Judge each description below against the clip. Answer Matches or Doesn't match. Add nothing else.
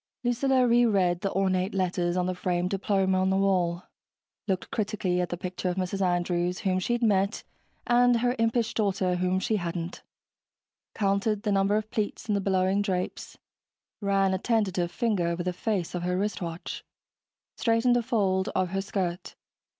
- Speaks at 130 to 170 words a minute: Matches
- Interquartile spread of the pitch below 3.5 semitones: Matches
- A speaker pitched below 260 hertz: Matches